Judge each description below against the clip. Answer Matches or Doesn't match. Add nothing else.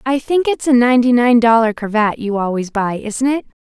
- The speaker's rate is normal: Doesn't match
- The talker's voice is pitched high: Matches